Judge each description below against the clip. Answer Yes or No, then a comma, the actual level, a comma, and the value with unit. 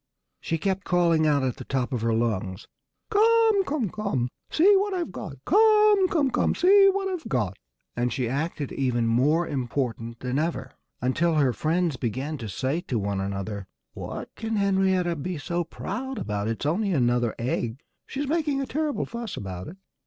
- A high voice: No, medium, 155 Hz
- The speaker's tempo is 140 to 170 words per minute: No, average, 180 wpm